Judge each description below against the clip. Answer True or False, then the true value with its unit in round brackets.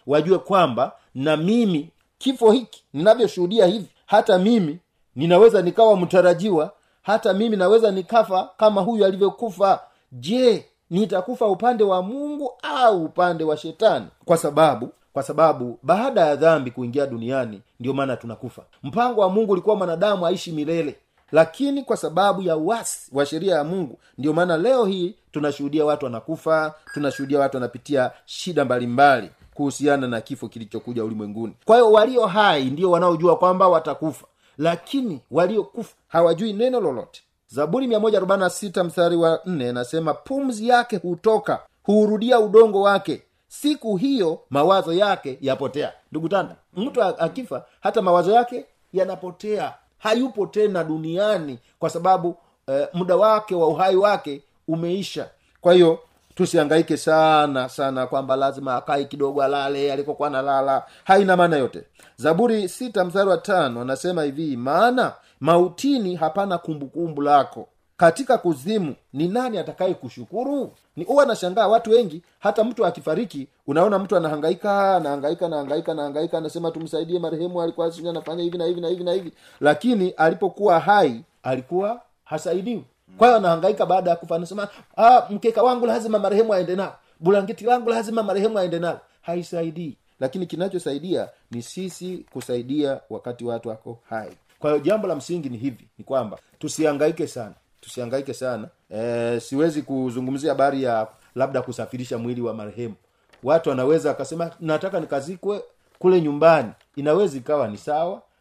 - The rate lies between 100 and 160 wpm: True (135 wpm)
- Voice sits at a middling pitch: True (170 Hz)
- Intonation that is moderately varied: False (5.9 semitones)